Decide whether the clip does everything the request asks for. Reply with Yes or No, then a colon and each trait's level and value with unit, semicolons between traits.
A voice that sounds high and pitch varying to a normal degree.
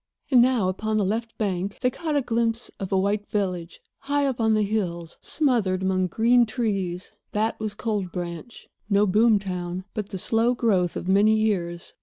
Yes: high, 210 Hz; average, 3.5 semitones